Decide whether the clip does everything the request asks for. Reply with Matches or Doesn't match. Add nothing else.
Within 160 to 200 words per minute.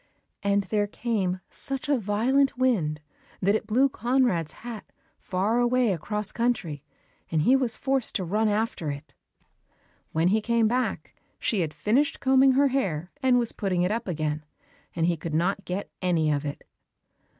Matches